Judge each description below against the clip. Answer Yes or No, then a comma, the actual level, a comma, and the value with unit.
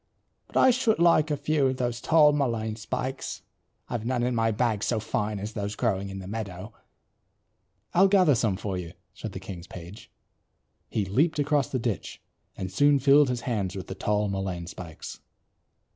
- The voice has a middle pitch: No, low, 115 Hz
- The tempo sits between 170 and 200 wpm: Yes, average, 180 wpm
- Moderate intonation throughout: No, wide, 6.1 semitones